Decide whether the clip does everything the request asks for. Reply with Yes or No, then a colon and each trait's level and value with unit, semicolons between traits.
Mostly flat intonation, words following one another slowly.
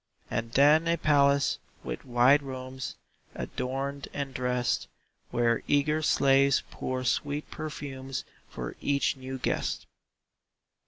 Yes: narrow, 1.9 semitones; slow, 110 wpm